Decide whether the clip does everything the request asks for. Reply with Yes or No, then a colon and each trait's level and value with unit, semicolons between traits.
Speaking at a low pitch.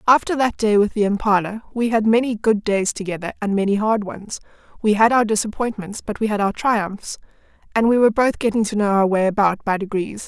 No: high, 210 Hz